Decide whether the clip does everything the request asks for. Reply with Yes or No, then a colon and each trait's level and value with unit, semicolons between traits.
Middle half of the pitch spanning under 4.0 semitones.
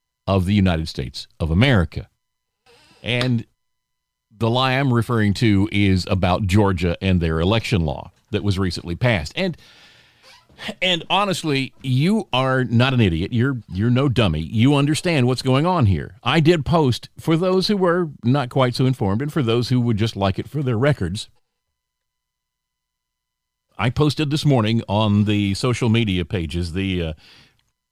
No: wide, 5.5 semitones